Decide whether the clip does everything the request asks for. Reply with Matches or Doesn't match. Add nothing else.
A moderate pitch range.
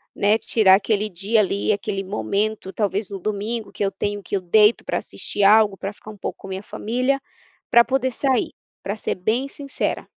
Doesn't match